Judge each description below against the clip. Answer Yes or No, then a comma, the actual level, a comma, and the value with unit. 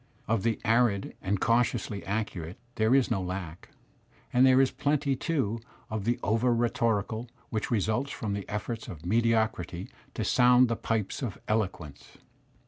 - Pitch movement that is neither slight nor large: Yes, average, 3.3 semitones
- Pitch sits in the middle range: No, low, 110 Hz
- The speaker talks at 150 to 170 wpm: Yes, average, 155 wpm